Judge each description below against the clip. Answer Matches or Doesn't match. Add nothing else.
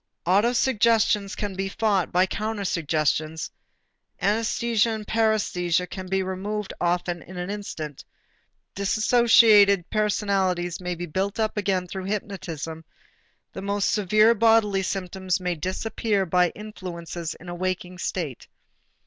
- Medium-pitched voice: Doesn't match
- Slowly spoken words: Matches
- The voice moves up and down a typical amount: Matches